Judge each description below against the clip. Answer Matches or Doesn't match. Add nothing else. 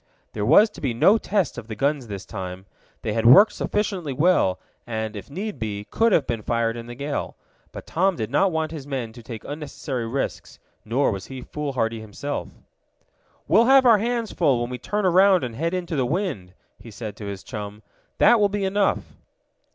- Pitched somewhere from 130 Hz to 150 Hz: Matches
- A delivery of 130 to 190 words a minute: Doesn't match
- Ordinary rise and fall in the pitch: Doesn't match